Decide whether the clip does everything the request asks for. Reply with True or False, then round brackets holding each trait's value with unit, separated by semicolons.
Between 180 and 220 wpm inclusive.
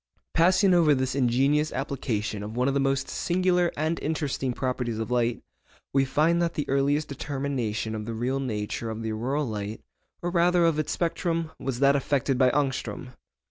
False (170 wpm)